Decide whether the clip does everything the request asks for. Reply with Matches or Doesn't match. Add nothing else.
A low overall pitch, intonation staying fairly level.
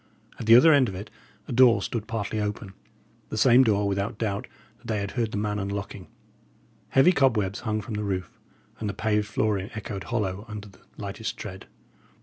Matches